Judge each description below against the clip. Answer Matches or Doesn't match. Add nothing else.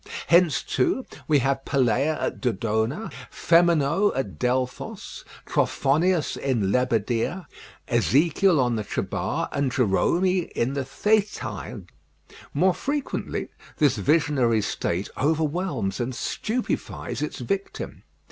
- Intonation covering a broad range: Matches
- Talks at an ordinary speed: Doesn't match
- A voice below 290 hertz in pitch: Matches